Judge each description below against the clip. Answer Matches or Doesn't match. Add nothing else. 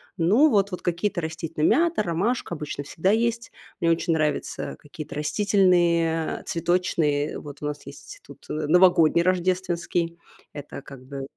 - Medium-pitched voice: Matches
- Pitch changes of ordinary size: Matches